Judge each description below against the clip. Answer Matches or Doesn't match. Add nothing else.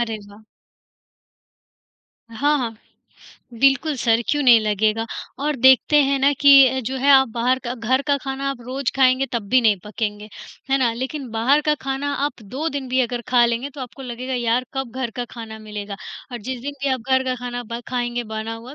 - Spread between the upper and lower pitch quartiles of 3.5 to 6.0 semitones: Doesn't match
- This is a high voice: Matches